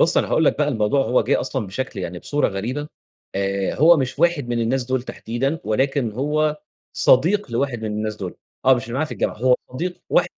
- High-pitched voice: No, low, 130 Hz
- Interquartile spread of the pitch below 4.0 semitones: No, average, 4.9 semitones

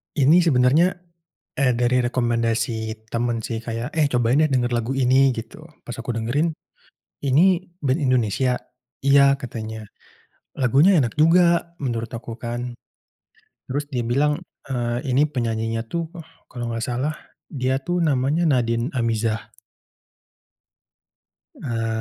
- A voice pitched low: Yes, low, 125 Hz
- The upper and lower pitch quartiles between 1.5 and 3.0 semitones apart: No, average, 3.4 semitones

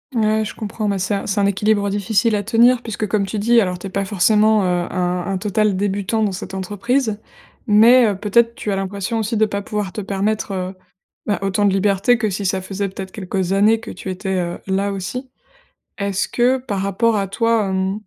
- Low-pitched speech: No, high, 200 Hz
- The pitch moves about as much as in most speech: No, narrow, 2.2 semitones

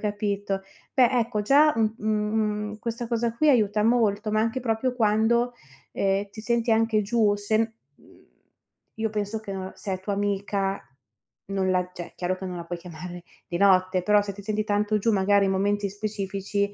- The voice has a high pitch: Yes, high, 210 Hz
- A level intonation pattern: Yes, narrow, 2.1 semitones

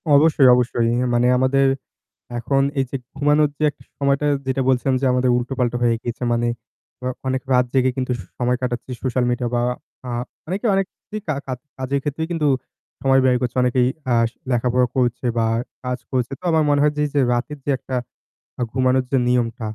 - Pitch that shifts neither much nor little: No, narrow, 2.1 semitones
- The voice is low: Yes, low, 130 Hz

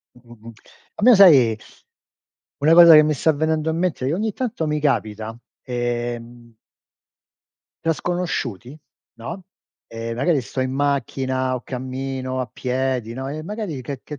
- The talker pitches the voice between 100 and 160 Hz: Yes, low, 135 Hz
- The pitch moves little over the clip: No, average, 4.6 semitones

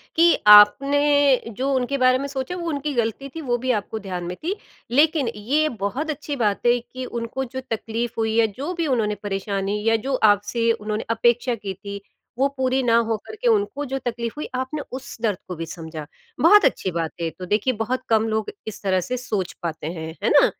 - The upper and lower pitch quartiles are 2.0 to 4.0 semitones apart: No, average, 4.9 semitones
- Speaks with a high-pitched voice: Yes, high, 235 Hz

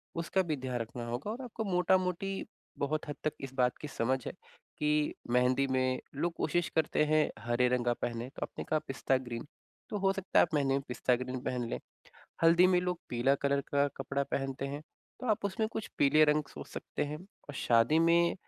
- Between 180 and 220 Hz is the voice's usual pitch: No, medium, 145 Hz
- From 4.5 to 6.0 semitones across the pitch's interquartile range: Yes, average, 5.1 semitones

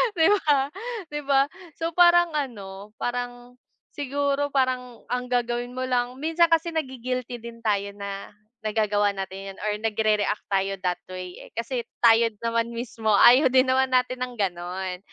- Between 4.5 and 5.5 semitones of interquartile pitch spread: No, average, 4.0 semitones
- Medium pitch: No, high, 245 Hz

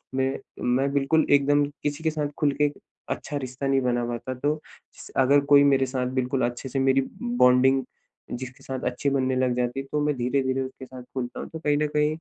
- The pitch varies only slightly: Yes, narrow, 2.0 semitones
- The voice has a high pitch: No, low, 135 Hz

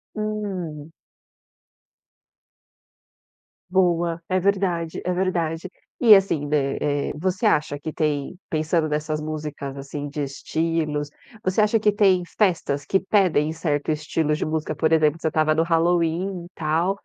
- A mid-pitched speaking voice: Yes, medium, 160 Hz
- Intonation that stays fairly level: No, average, 3.5 semitones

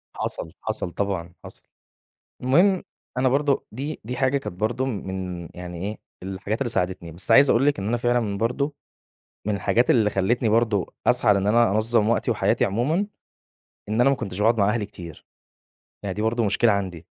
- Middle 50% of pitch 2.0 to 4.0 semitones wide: No, average, 4.4 semitones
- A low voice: Yes, low, 110 Hz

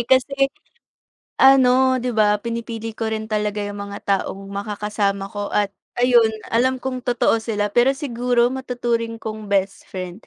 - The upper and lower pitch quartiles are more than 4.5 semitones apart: No, average, 3.2 semitones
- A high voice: Yes, high, 225 Hz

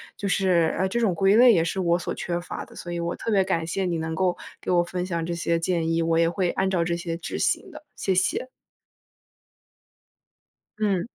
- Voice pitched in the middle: Yes, medium, 175 Hz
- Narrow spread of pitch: Yes, narrow, 2.2 semitones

